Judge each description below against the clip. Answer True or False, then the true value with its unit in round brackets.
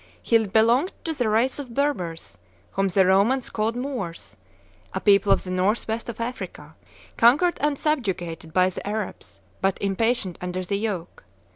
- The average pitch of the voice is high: True (215 Hz)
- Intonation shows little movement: False (4.8 semitones)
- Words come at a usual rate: True (160 wpm)